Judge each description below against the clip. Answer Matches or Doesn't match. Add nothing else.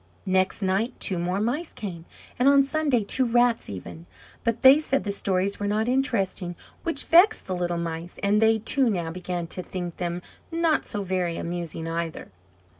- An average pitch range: Doesn't match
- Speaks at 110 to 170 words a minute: Doesn't match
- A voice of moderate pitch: Doesn't match